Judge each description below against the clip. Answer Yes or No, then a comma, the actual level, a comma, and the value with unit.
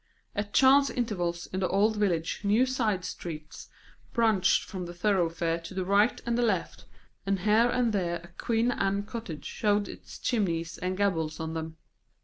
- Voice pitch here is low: No, high, 195 Hz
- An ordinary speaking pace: Yes, average, 170 wpm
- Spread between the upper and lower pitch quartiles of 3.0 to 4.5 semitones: Yes, average, 4.2 semitones